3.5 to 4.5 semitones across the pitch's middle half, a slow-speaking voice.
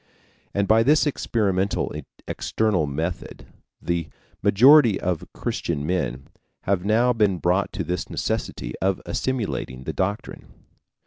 Yes: average, 4.2 semitones; slow, 120 wpm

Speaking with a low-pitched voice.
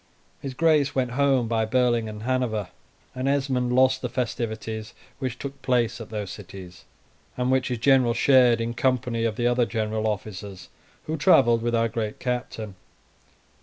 Yes: low, 120 Hz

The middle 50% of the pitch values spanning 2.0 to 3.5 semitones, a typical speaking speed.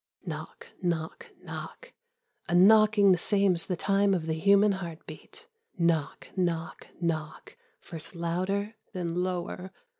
No: average, 2.9 semitones; slow, 125 wpm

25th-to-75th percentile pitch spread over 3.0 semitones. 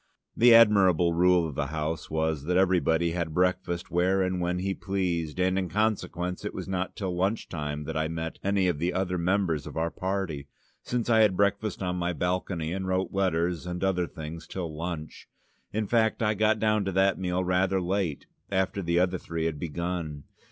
No: narrow, 2.6 semitones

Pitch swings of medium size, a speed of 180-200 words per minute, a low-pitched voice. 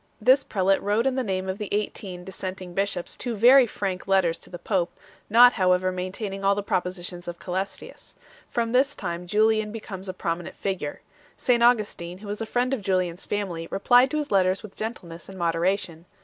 No: average, 3.3 semitones; average, 190 wpm; high, 195 Hz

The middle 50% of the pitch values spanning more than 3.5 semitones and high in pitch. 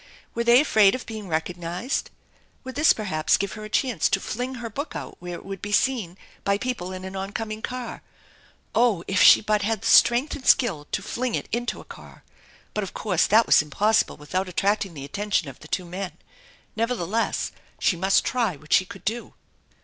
Yes: average, 4.3 semitones; high, 205 Hz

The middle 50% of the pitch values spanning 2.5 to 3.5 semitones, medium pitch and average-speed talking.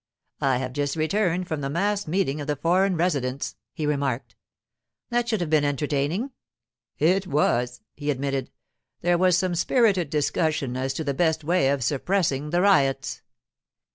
No: average, 4.6 semitones; medium, 155 Hz; average, 160 wpm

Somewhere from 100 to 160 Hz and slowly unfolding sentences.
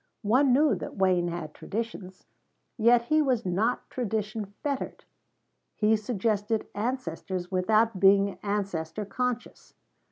No: high, 210 Hz; slow, 115 wpm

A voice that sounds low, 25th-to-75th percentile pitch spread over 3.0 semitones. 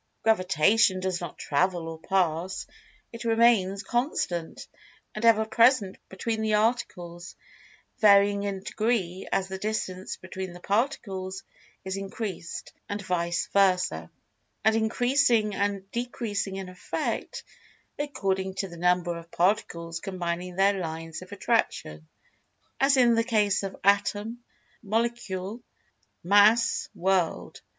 No: high, 195 Hz; average, 3.4 semitones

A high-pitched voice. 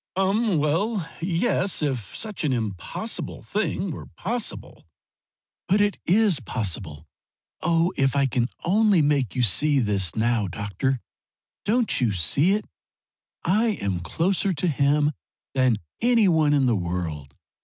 No: medium, 150 Hz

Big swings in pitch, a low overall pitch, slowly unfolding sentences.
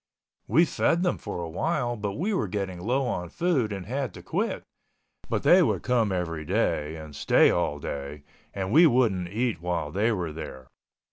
No: wide, 7.1 semitones; low, 100 Hz; average, 185 wpm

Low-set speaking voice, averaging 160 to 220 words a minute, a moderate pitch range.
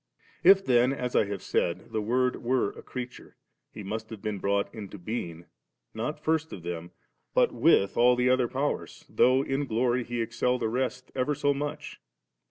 Yes: low, 120 Hz; average, 180 wpm; average, 3.3 semitones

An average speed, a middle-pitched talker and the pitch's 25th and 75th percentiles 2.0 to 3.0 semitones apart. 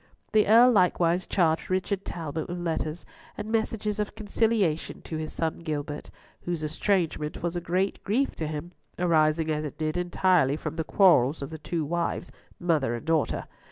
No: average, 170 wpm; medium, 170 Hz; average, 3.4 semitones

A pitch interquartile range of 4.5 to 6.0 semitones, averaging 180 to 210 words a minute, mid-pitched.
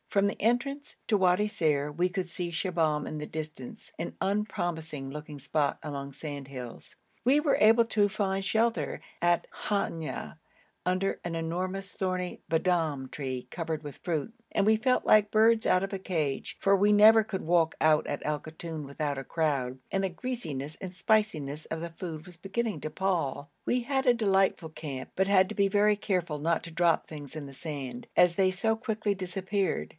Yes: average, 4.8 semitones; average, 185 wpm; medium, 175 Hz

